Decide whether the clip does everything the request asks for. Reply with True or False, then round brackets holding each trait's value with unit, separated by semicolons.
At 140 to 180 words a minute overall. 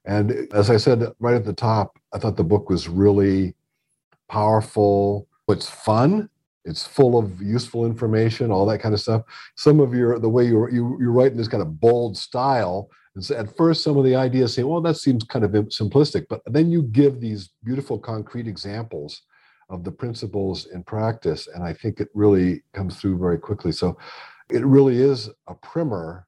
False (190 wpm)